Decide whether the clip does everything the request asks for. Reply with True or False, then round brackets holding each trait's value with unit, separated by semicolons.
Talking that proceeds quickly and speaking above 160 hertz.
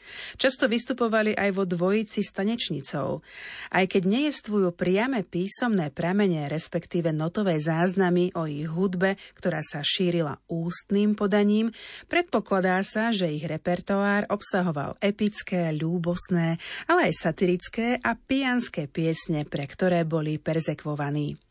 False (115 wpm; 185 Hz)